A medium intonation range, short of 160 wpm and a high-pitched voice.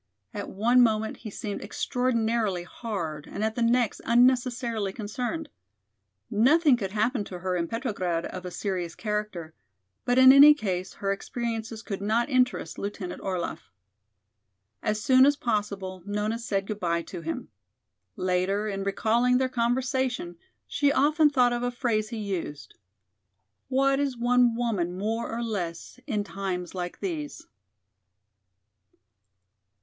Yes: average, 4.2 semitones; average, 140 wpm; high, 220 Hz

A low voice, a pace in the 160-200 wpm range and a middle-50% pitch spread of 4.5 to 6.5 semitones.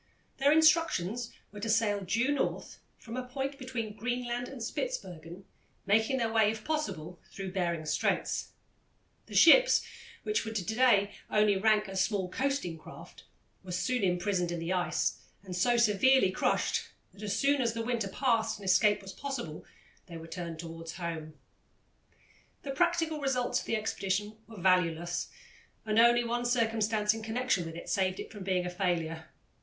No: high, 215 Hz; average, 165 wpm; average, 5.1 semitones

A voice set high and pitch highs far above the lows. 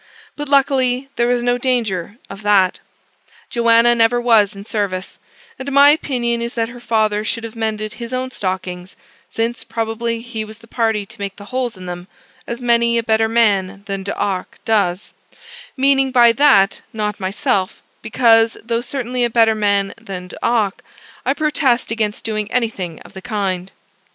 No: high, 225 Hz; average, 3.1 semitones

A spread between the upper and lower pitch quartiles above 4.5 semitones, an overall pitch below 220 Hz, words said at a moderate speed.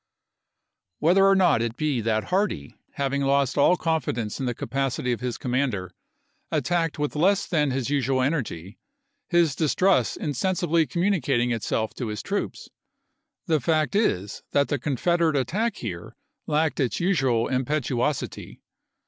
Yes: average, 5.3 semitones; medium, 140 Hz; average, 145 wpm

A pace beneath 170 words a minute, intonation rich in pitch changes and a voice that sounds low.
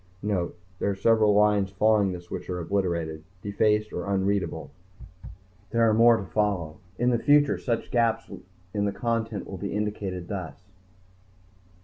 No: average, 150 wpm; average, 2.7 semitones; low, 100 Hz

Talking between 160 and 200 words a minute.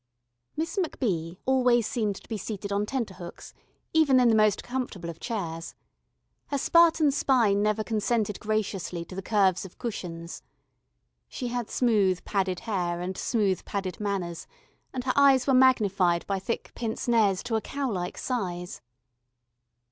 No: average, 150 wpm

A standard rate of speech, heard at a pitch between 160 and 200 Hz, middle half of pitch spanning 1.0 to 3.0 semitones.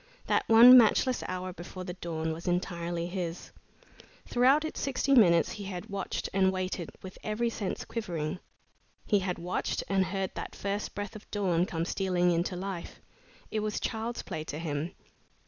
No: average, 165 wpm; medium, 185 Hz; average, 3.5 semitones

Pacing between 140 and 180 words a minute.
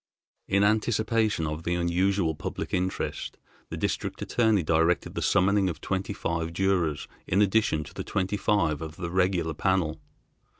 Yes: average, 155 wpm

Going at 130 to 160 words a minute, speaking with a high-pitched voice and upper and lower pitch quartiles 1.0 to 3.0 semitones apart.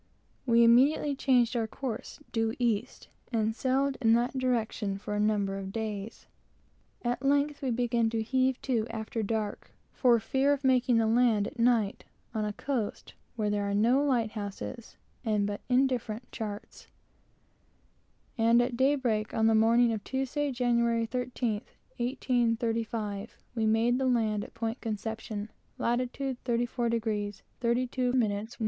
Yes: average, 145 wpm; high, 230 Hz; narrow, 2.5 semitones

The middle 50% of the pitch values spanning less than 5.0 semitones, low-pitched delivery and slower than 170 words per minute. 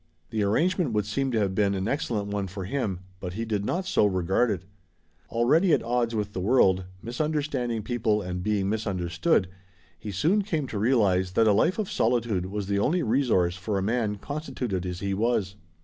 No: average, 4.3 semitones; low, 105 Hz; average, 195 wpm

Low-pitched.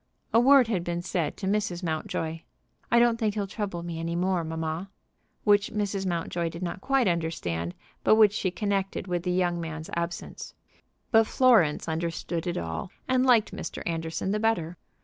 No: medium, 180 Hz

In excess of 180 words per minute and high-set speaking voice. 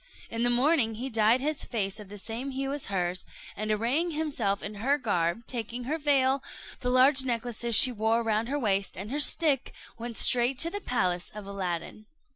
Yes: average, 195 wpm; high, 235 Hz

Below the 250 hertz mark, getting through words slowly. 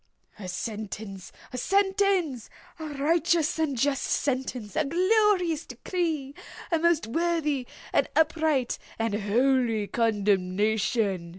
No: very high, 275 Hz; slow, 85 wpm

